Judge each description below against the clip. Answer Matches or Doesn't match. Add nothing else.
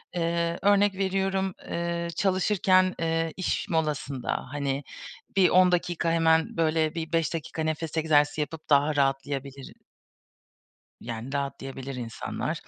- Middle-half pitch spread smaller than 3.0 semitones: Doesn't match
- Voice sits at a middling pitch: Matches